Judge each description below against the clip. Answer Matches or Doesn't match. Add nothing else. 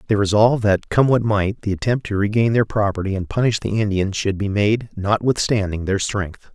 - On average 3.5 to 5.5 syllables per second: Matches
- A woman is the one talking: Doesn't match